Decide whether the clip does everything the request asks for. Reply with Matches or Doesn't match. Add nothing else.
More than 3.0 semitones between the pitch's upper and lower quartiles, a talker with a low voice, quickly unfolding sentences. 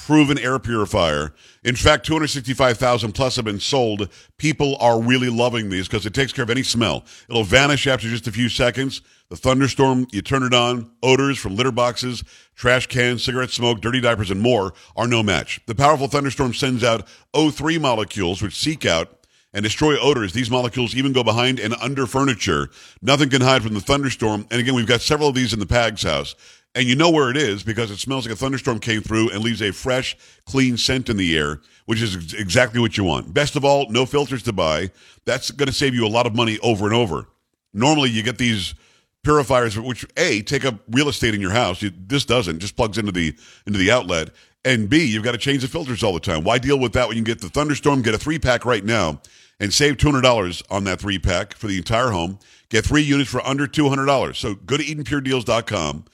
Matches